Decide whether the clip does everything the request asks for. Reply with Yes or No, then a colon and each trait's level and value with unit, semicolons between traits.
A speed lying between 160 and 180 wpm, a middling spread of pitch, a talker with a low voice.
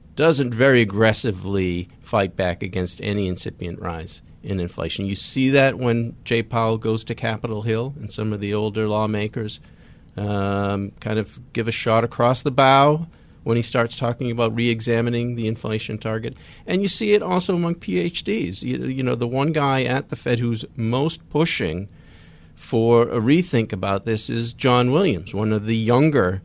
Yes: average, 170 wpm; average, 3.5 semitones; low, 115 Hz